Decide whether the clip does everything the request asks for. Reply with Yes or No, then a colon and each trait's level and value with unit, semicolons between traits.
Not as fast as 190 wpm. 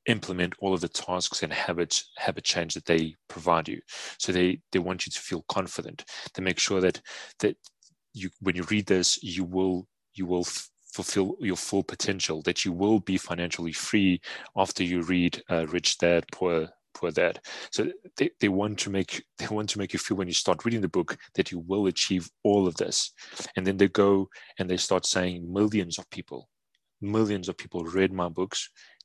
No: average, 200 wpm